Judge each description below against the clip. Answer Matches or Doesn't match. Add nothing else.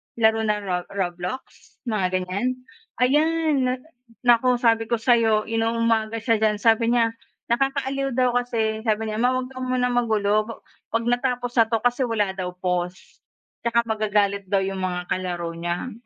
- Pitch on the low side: Doesn't match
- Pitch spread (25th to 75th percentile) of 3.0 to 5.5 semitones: Matches